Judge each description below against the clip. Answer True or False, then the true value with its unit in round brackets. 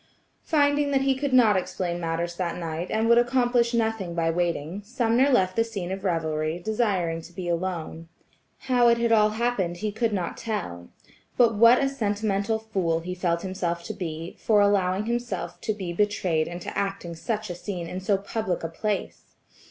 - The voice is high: True (195 Hz)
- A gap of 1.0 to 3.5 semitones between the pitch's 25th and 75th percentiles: False (4.8 semitones)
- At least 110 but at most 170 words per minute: False (185 wpm)